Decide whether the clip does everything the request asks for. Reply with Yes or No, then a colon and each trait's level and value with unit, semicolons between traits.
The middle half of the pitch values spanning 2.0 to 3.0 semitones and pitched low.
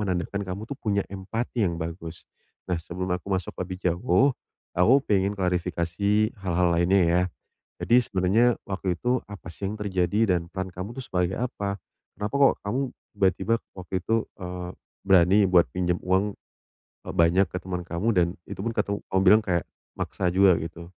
Yes: narrow, 2.6 semitones; very low, 95 Hz